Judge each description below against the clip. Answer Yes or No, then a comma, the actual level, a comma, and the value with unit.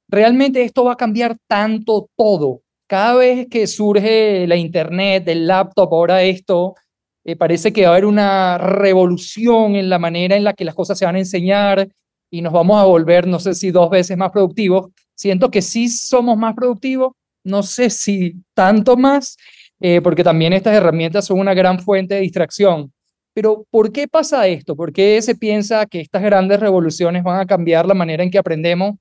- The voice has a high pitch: Yes, high, 195 Hz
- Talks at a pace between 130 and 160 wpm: No, fast, 190 wpm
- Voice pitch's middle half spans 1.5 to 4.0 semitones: Yes, average, 3.4 semitones